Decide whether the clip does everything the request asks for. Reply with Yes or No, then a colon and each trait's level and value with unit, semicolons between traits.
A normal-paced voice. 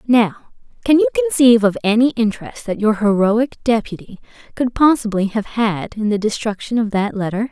Yes: average, 170 wpm